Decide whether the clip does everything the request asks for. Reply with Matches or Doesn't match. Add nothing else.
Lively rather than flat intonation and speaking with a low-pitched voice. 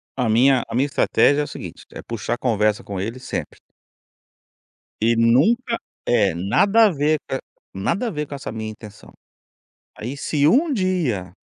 Matches